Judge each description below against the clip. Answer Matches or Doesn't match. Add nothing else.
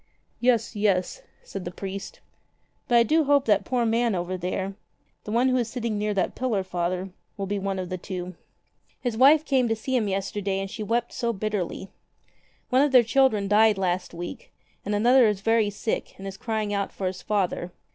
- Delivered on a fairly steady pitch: Doesn't match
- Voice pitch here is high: Matches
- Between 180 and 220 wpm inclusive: Matches